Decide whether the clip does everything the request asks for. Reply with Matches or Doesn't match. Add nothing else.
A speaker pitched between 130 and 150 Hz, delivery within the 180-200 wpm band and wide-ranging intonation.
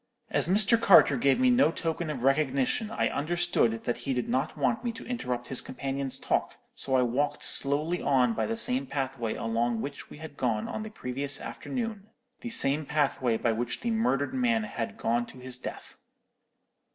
Matches